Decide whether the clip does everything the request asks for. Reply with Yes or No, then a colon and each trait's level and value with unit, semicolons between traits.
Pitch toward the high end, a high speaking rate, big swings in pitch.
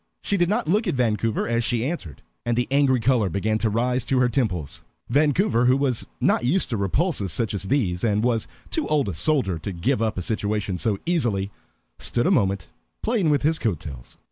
No: low, 120 Hz; fast, 210 wpm; wide, 5.7 semitones